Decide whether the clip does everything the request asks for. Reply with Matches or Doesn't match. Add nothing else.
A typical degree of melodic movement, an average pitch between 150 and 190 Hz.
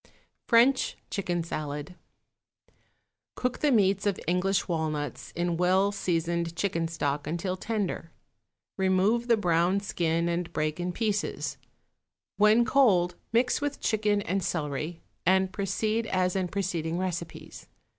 Matches